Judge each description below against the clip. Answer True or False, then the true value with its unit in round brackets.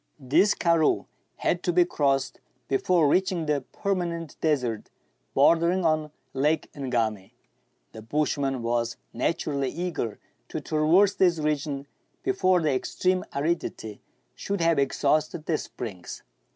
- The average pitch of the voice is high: False (155 Hz)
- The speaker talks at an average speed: False (125 wpm)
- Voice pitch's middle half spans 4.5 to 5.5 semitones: False (4.0 semitones)